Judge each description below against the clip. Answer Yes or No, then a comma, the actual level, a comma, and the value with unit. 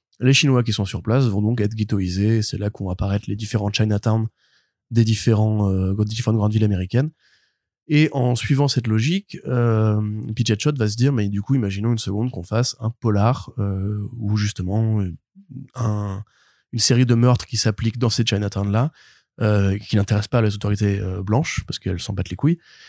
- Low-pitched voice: Yes, low, 110 Hz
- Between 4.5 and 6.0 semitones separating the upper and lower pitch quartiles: No, average, 3.0 semitones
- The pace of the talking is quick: No, average, 185 wpm